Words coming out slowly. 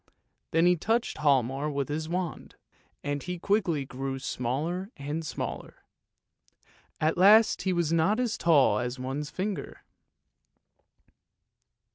Yes: slow, 125 wpm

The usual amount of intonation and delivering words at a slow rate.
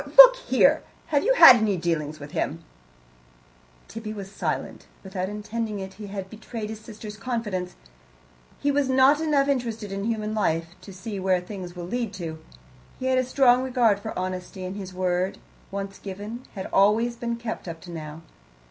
No: average, 4.2 semitones; average, 180 wpm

